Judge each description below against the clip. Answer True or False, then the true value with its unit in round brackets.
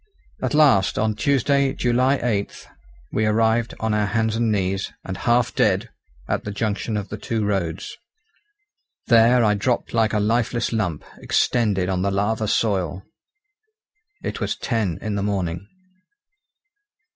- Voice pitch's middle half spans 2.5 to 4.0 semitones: True (2.9 semitones)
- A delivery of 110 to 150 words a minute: True (145 wpm)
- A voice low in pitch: True (110 Hz)